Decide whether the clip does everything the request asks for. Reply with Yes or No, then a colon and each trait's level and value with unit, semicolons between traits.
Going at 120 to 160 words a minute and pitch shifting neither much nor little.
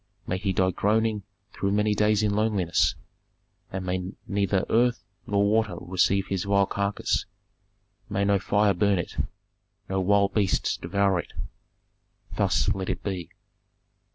No: average, 140 wpm; narrow, 1.6 semitones